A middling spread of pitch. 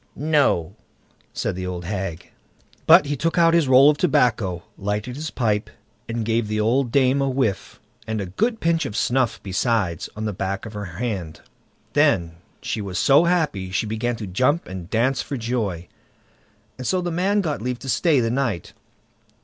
No: wide, 6.0 semitones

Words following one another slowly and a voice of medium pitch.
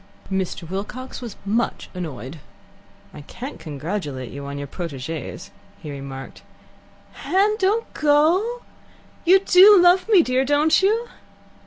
No: slow, 125 wpm; high, 240 Hz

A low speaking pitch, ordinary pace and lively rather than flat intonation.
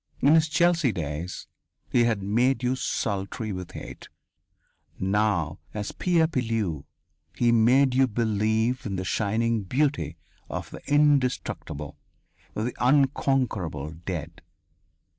No: low, 110 Hz; slow, 115 wpm; wide, 5.8 semitones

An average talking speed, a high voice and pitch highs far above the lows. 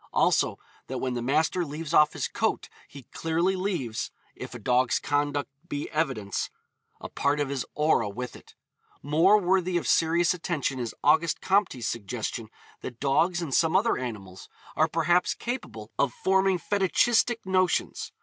No: average, 155 wpm; medium, 155 Hz; wide, 5.9 semitones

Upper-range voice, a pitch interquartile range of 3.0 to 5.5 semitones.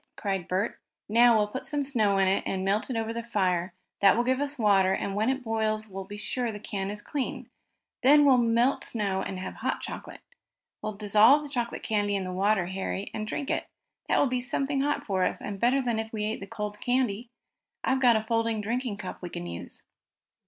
Yes: high, 215 Hz; average, 3.8 semitones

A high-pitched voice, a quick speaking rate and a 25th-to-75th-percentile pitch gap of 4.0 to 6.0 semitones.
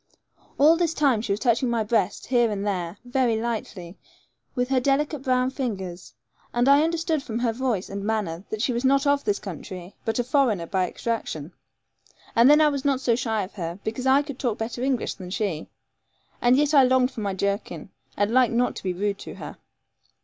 Yes: high, 235 Hz; fast, 210 wpm; average, 4.8 semitones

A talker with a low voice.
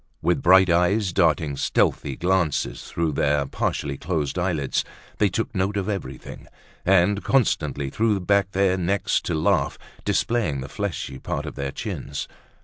Yes: very low, 90 Hz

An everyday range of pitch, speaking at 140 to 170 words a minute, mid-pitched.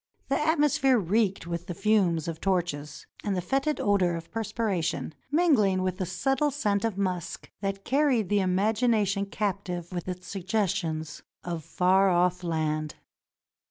No: average, 3.8 semitones; average, 145 wpm; high, 195 Hz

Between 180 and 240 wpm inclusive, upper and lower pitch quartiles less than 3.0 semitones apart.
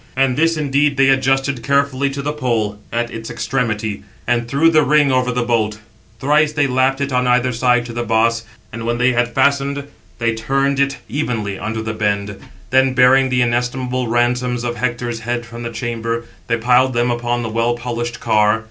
Yes: average, 190 wpm; narrow, 2.5 semitones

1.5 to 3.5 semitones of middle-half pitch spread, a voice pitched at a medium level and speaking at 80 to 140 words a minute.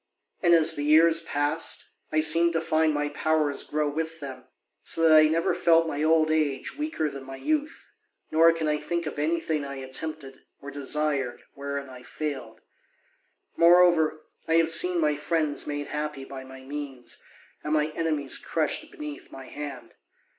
No: narrow, 2.4 semitones; medium, 155 Hz; average, 170 wpm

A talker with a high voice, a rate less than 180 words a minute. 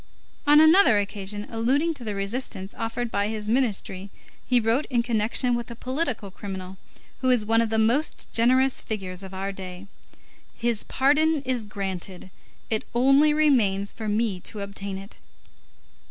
Yes: high, 225 Hz; average, 155 wpm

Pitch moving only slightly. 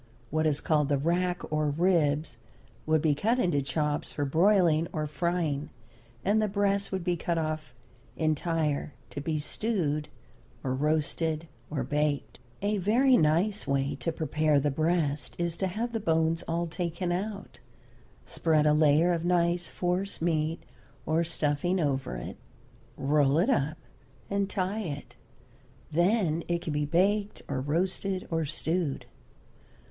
No: average, 3.2 semitones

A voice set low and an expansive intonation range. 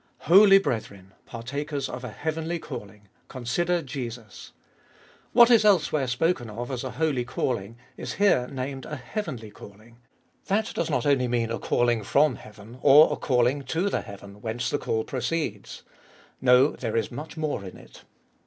No: low, 130 Hz; average, 5.0 semitones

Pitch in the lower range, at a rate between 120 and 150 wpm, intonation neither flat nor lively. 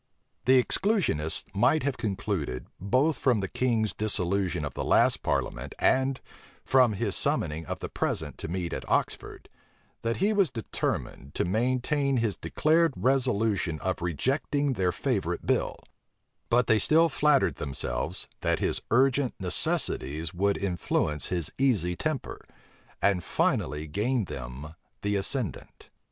No: low, 105 Hz; slow, 135 wpm; wide, 7.0 semitones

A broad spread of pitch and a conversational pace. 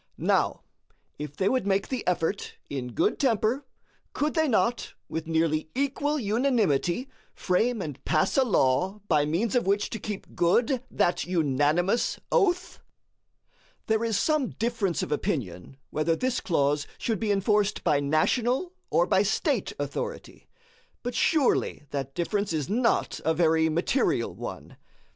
Yes: wide, 7.3 semitones; average, 145 wpm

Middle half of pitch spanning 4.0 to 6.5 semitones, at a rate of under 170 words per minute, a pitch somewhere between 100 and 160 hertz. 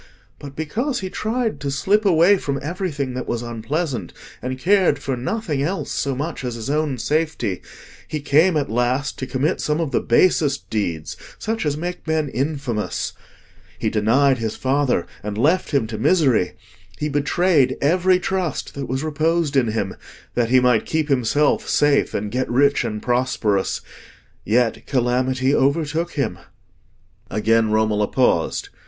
Yes: average, 4.6 semitones; average, 155 wpm; medium, 140 Hz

